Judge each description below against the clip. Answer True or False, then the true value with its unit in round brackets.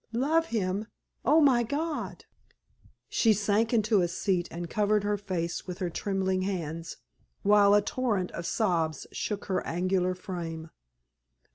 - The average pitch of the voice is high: True (195 Hz)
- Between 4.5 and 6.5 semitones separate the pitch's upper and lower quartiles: False (3.3 semitones)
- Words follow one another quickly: False (140 wpm)